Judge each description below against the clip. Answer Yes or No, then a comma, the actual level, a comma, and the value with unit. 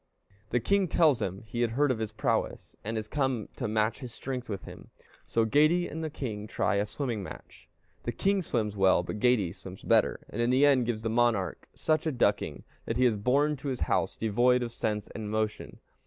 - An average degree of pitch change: Yes, average, 3.9 semitones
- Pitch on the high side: No, low, 120 Hz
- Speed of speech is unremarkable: No, fast, 215 wpm